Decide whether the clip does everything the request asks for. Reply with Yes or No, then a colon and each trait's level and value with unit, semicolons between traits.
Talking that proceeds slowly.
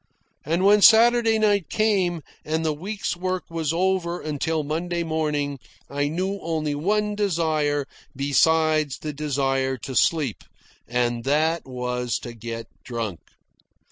Yes: slow, 130 wpm